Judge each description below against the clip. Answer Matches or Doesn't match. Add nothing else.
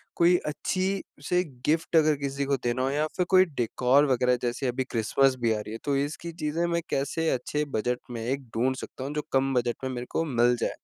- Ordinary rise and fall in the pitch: Matches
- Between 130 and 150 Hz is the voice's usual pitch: Matches